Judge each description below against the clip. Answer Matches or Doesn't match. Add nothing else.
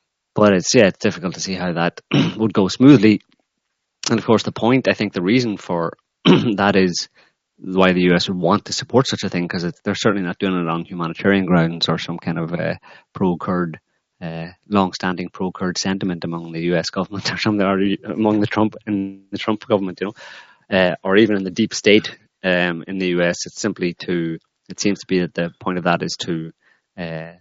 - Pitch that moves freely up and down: Doesn't match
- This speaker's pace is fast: Matches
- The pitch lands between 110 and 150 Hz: Doesn't match